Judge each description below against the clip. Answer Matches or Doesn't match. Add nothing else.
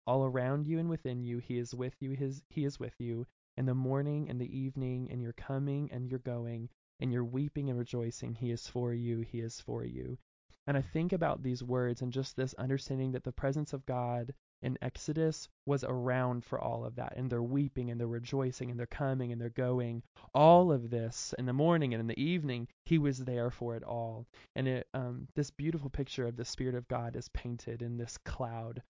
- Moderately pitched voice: Doesn't match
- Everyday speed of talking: Doesn't match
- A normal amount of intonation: Doesn't match